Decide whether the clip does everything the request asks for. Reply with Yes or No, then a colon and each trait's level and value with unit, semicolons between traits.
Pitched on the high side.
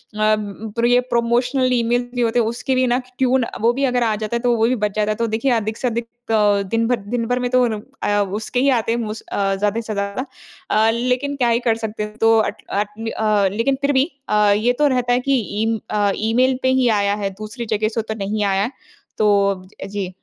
Yes: high, 230 Hz